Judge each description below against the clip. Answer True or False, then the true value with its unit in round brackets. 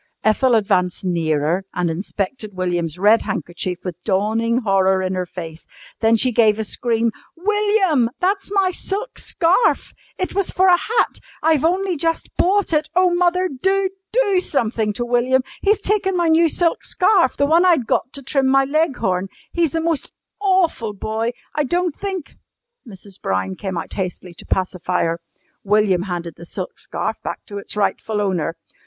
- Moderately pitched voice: False (240 Hz)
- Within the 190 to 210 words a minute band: False (170 wpm)